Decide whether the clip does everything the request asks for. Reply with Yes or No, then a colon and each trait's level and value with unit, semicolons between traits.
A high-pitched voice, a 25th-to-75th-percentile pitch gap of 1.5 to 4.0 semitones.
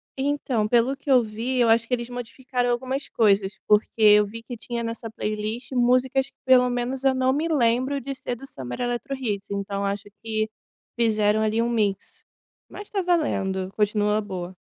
Yes: high, 235 Hz; average, 3.6 semitones